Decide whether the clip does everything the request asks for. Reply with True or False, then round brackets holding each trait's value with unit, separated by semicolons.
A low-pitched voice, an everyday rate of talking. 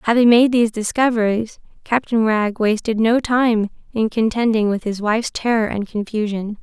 False (225 Hz; 155 wpm)